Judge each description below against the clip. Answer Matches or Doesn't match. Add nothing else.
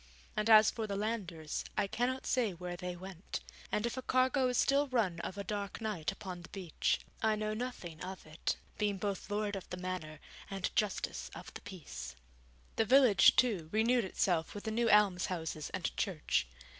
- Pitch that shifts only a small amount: Doesn't match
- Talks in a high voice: Matches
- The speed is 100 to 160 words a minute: Doesn't match